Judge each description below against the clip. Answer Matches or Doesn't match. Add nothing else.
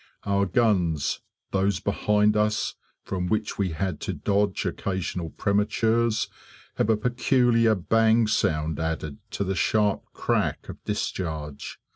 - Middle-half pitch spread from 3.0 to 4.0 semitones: Matches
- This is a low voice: Matches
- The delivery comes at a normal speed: Doesn't match